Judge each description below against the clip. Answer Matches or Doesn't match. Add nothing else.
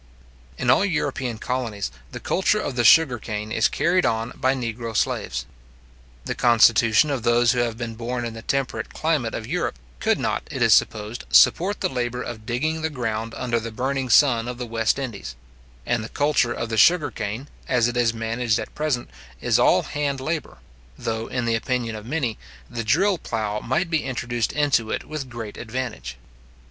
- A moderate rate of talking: Matches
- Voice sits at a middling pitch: Doesn't match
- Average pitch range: Matches